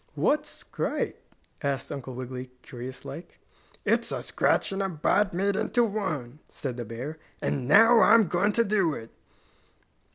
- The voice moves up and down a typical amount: No, wide, 7.9 semitones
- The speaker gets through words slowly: No, average, 155 wpm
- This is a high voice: No, medium, 165 Hz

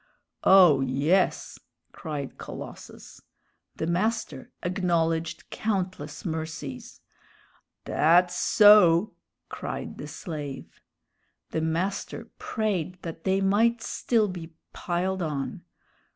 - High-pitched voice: No, medium, 175 Hz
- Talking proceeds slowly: Yes, slow, 90 wpm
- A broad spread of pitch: No, average, 3.3 semitones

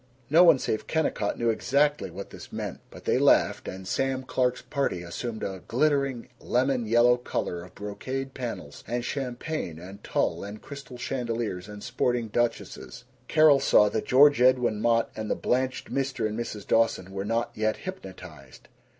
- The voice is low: Yes, low, 120 Hz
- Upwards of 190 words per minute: No, average, 165 wpm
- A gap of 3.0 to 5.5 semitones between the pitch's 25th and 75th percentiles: Yes, average, 4.1 semitones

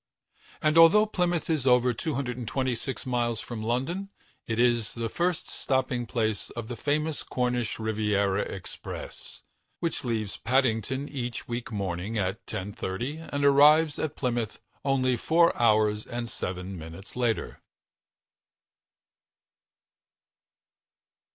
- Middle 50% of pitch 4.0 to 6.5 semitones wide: Yes, average, 4.4 semitones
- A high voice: No, low, 120 Hz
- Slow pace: Yes, slow, 110 wpm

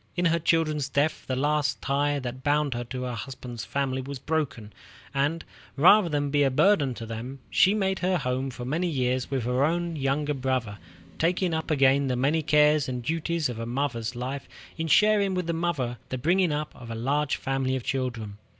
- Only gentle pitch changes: No, average, 3.9 semitones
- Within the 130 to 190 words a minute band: No, average, 200 wpm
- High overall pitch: No, medium, 140 Hz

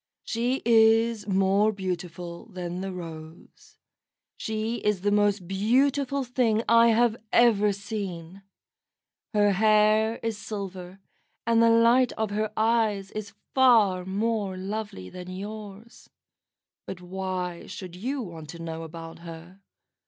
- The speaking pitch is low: No, high, 205 Hz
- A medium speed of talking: No, slow, 125 wpm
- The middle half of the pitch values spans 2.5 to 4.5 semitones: Yes, average, 3.7 semitones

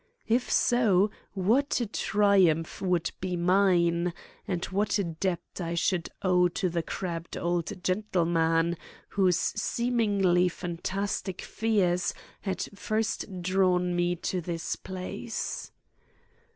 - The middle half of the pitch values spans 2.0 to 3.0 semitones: Yes, narrow, 2.5 semitones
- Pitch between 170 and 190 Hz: Yes, medium, 185 Hz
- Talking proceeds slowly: Yes, slow, 110 wpm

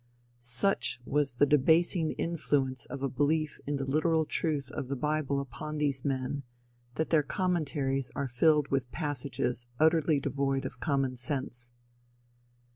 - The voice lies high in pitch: No, medium, 140 Hz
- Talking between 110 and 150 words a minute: Yes, average, 140 wpm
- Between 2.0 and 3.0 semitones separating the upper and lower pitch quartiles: Yes, narrow, 2.6 semitones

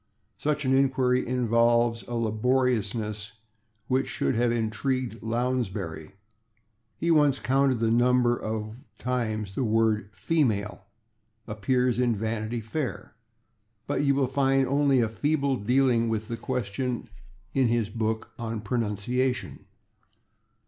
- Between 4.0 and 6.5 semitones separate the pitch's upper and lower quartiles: No, average, 2.9 semitones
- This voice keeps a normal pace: No, slow, 120 wpm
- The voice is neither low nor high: No, low, 120 Hz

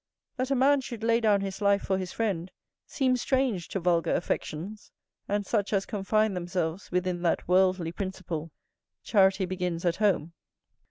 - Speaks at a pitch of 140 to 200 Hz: Yes, high, 190 Hz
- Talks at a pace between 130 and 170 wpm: Yes, average, 160 wpm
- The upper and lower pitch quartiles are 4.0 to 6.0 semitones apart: No, average, 3.3 semitones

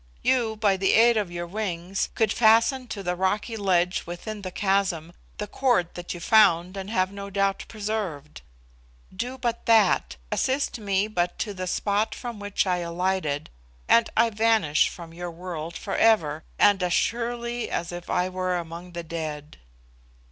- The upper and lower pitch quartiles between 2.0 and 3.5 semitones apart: No, average, 4.0 semitones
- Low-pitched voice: No, high, 195 Hz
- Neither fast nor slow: Yes, average, 170 wpm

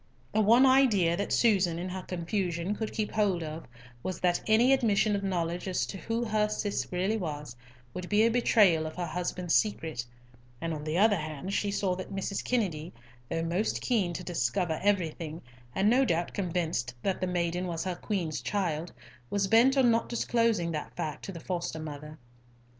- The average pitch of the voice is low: No, medium, 185 Hz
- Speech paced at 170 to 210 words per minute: Yes, average, 185 wpm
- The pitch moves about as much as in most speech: Yes, average, 4.1 semitones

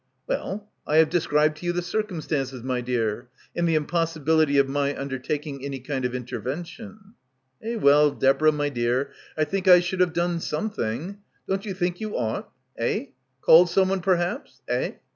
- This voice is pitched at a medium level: Yes, medium, 155 Hz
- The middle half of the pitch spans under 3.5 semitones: No, average, 4.6 semitones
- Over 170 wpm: Yes, average, 180 wpm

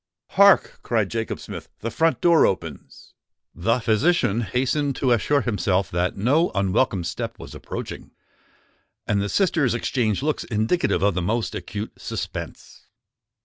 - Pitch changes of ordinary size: No, wide, 5.8 semitones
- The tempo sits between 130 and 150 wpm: Yes, average, 140 wpm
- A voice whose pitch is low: Yes, low, 115 Hz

